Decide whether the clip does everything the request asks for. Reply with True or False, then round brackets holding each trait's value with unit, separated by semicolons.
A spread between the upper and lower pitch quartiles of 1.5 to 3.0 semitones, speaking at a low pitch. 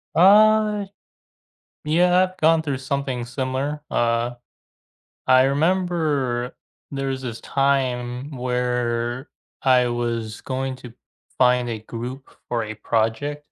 False (3.4 semitones; 130 Hz)